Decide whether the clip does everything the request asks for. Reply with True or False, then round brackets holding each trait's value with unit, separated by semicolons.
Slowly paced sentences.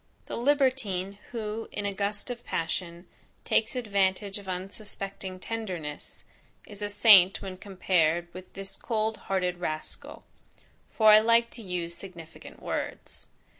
True (130 wpm)